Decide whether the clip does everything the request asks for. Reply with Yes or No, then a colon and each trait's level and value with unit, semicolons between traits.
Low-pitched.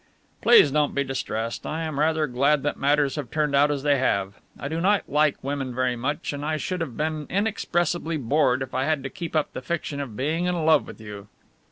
No: medium, 145 Hz